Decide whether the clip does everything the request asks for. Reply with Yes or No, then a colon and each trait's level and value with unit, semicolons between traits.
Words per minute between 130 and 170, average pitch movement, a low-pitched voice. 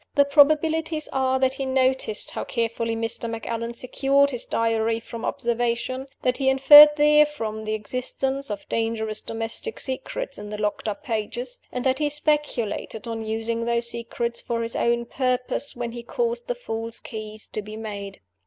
No: average, 165 wpm; average, 3.2 semitones; high, 235 Hz